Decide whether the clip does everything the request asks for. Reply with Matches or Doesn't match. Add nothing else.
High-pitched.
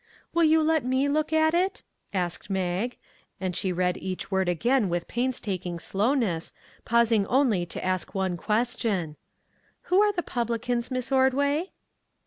Matches